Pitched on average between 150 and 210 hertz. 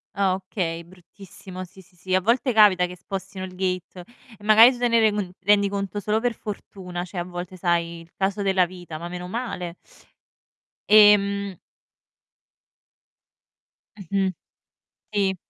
Yes: high, 190 Hz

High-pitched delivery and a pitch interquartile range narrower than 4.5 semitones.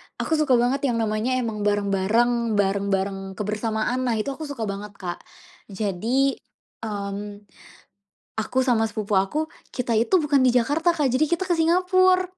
No: high, 230 Hz; average, 5.1 semitones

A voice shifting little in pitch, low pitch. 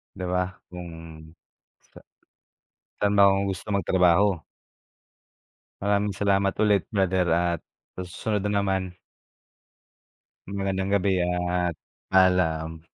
Yes: narrow, 2.0 semitones; very low, 95 Hz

